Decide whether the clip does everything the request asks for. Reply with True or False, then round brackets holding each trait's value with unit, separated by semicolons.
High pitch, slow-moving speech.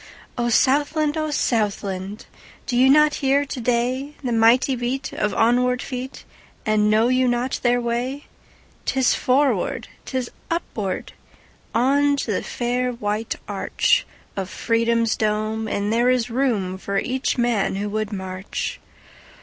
True (240 Hz; 115 wpm)